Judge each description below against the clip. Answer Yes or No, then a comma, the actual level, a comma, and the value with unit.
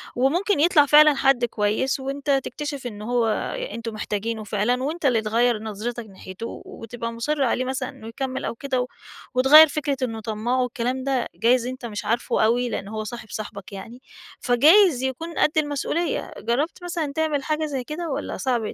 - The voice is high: Yes, very high, 255 Hz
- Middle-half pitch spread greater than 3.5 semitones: Yes, average, 4.1 semitones